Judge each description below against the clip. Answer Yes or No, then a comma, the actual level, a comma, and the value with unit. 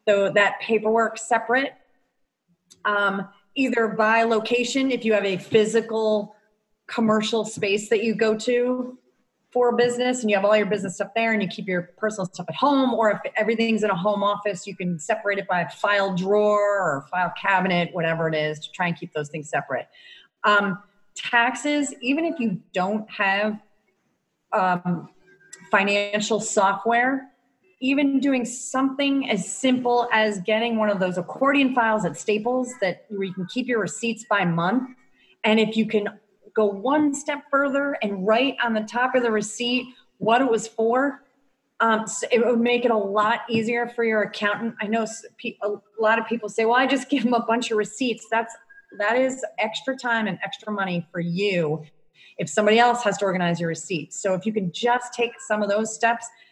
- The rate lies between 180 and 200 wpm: Yes, average, 185 wpm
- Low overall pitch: No, high, 220 Hz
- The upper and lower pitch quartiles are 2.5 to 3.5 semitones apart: Yes, average, 3.1 semitones